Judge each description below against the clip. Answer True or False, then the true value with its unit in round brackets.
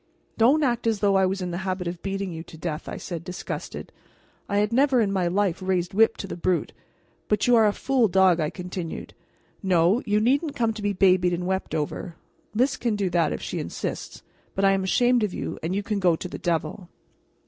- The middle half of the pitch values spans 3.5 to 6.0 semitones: False (3.1 semitones)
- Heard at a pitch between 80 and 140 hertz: False (190 Hz)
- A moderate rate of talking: False (225 wpm)